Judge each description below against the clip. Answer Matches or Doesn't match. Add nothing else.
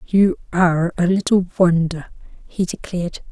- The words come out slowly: Matches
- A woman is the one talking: Matches